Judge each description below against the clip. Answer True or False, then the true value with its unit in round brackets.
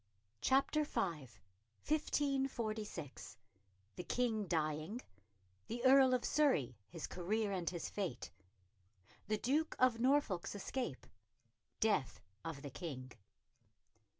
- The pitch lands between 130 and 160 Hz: False (210 Hz)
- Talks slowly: True (100 wpm)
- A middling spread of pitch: False (8.9 semitones)